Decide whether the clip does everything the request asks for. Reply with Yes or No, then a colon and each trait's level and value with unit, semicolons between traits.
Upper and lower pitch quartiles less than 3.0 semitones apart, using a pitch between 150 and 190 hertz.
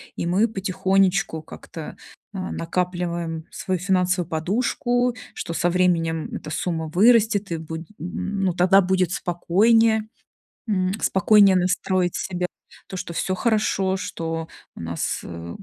Yes: narrow, 2.6 semitones; medium, 185 Hz